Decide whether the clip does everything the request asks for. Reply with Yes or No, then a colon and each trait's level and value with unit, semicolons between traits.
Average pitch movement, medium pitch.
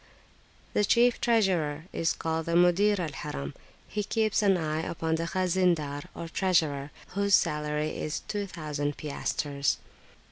Yes: average, 4.2 semitones; medium, 165 Hz